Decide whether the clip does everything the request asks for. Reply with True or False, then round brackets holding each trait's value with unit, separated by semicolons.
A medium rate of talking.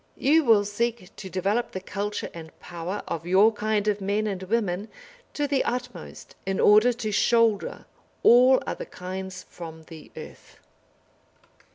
True (150 wpm)